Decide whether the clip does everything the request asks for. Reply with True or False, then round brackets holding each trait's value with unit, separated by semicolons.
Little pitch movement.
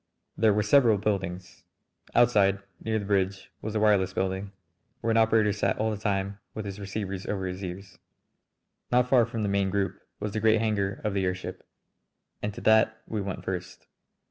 True (2.2 semitones)